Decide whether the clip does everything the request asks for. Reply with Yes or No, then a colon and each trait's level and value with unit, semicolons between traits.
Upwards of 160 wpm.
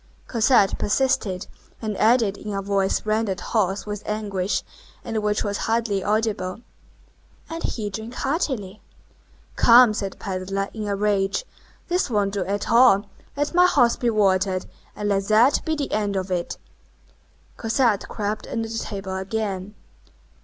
No: average, 150 wpm